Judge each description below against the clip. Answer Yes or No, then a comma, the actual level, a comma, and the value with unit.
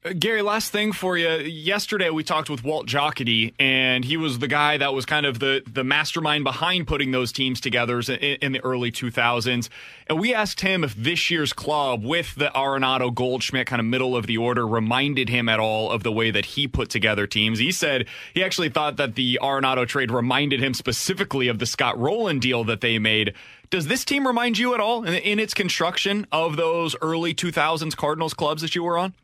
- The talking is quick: Yes, fast, 215 wpm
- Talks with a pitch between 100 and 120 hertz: No, medium, 140 Hz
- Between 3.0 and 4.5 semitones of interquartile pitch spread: No, average, 5.0 semitones